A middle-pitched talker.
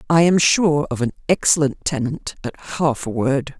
Yes: medium, 145 Hz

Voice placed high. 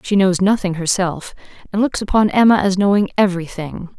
Yes: high, 195 Hz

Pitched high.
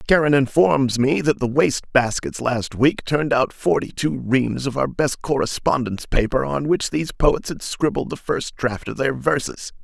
No: low, 135 Hz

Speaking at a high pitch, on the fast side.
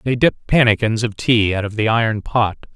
No: low, 110 Hz; fast, 215 wpm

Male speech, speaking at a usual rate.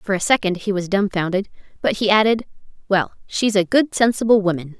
No: female; average, 190 wpm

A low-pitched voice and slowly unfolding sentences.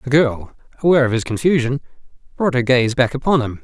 No: low, 130 Hz; average, 200 wpm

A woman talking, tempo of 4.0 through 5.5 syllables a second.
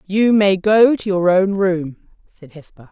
No: female; 3.8 syllables/s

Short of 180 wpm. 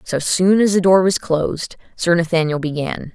No: average, 190 wpm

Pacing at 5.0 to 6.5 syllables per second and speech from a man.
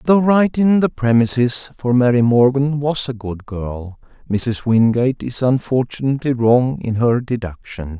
No: 4.4 syllables/s; male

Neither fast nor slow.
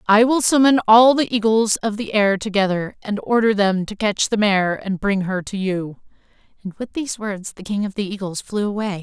No: fast, 220 wpm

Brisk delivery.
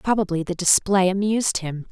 No: average, 155 wpm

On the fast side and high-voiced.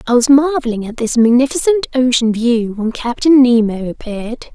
No: average, 160 wpm; high, 245 Hz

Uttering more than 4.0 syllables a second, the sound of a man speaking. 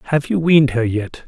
Yes: 5.8 syllables/s; male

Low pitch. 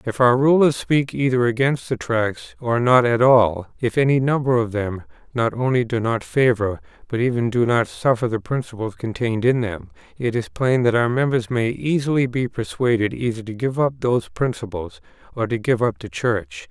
Yes: low, 120 Hz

